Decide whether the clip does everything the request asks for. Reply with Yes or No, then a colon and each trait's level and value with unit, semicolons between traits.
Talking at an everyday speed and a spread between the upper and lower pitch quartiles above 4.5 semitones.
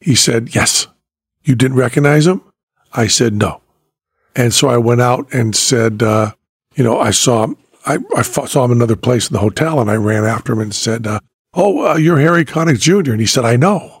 No: fast, 220 wpm; average, 4.9 semitones